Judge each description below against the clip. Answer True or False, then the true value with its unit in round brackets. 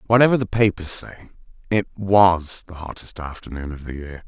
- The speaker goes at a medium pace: True (170 wpm)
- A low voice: True (90 Hz)